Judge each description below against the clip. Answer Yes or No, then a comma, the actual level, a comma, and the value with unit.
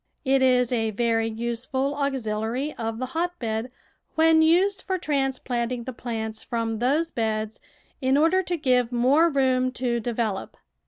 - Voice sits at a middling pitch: No, very high, 250 Hz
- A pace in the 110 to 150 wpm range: Yes, average, 145 wpm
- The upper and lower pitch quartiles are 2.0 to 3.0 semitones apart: No, average, 3.7 semitones